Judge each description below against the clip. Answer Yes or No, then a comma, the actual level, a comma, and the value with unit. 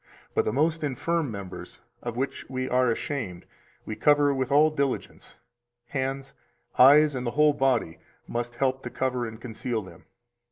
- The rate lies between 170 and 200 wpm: No, average, 160 wpm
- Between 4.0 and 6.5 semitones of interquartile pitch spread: No, average, 3.1 semitones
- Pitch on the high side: No, low, 130 Hz